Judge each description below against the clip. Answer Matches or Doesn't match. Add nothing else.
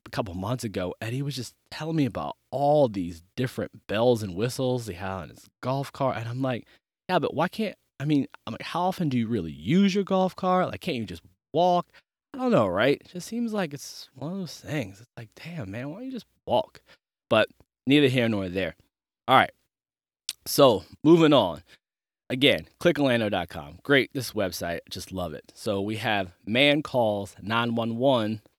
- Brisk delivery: Doesn't match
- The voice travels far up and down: Matches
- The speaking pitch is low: Matches